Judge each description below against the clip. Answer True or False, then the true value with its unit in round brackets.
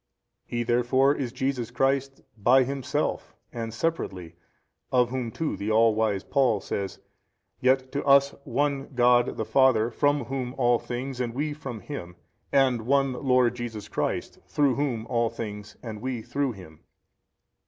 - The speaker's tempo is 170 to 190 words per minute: False (160 wpm)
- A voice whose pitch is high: False (125 Hz)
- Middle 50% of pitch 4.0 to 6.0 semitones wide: False (3.2 semitones)